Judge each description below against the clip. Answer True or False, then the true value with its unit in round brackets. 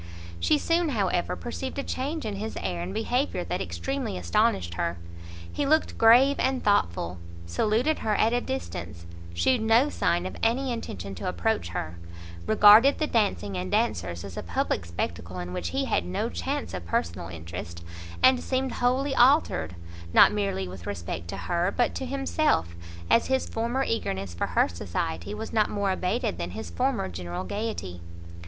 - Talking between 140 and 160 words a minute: False (170 wpm)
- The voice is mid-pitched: True (175 Hz)